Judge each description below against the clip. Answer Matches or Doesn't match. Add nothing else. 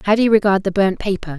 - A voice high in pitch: Matches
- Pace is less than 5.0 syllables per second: Doesn't match